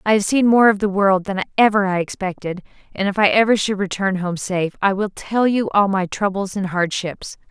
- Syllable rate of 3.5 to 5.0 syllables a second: No, 5.3 syllables/s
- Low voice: No, high, 195 Hz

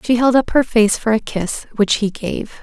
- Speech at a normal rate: No, fast, 250 wpm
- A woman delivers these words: Yes, female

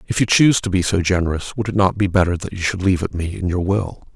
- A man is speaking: Yes, male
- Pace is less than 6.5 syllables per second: No, 6.6 syllables/s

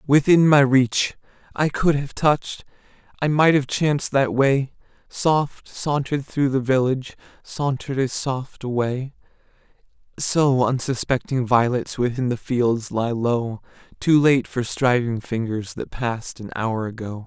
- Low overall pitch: Yes, low, 130 Hz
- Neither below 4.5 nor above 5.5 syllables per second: No, 4.2 syllables/s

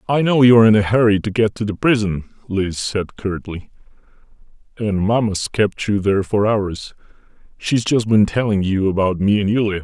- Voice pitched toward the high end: No, low, 105 Hz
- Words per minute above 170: Yes, average, 190 wpm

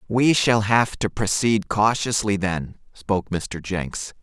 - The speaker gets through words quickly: No, average, 140 wpm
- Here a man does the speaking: Yes, male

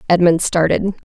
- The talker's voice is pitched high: No, medium, 175 Hz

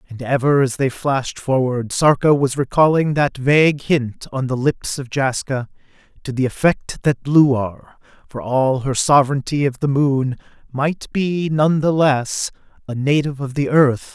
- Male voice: Yes, male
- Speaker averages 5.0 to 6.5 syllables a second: No, 4.5 syllables/s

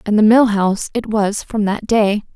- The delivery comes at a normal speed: No, fast, 230 wpm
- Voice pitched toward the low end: No, high, 210 Hz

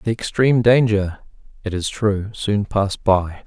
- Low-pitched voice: Yes, low, 105 Hz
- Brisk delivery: No, average, 155 wpm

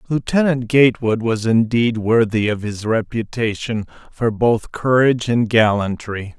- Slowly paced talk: Yes, slow, 120 wpm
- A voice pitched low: Yes, low, 115 Hz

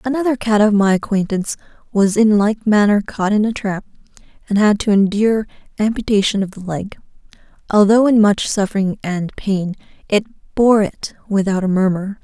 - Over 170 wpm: No, average, 160 wpm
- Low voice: No, high, 205 Hz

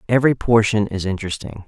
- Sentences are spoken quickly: No, average, 145 wpm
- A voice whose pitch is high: No, low, 105 Hz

